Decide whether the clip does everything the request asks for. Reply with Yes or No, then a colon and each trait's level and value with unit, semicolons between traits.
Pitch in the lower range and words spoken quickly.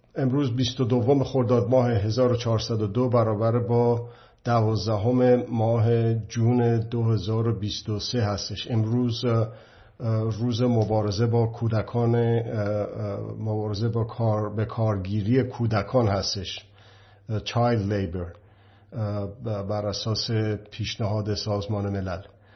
No: low, 110 Hz; slow, 85 wpm